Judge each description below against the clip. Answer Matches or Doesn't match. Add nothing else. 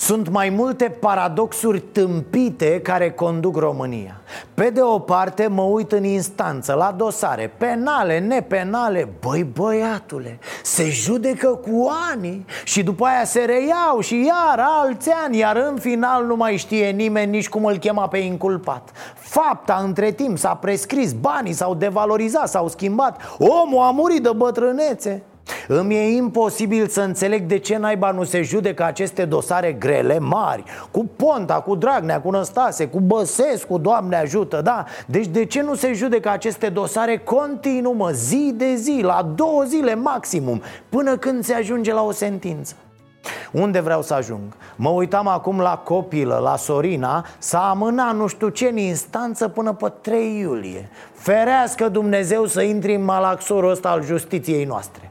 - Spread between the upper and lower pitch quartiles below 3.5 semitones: Doesn't match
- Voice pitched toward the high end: Matches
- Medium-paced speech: Matches